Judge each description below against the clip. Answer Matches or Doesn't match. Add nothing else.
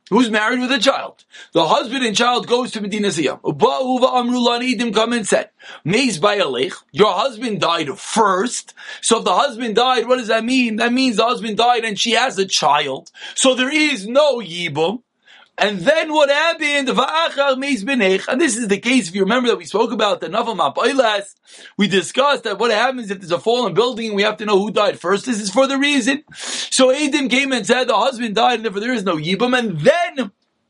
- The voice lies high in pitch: Matches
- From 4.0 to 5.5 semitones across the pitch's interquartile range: Doesn't match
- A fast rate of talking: Matches